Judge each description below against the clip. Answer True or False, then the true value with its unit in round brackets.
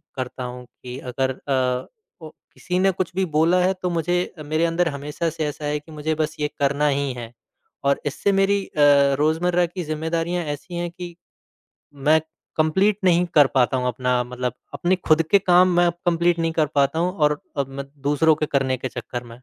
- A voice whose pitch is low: False (155 Hz)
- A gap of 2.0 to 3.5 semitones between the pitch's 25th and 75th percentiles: False (4.2 semitones)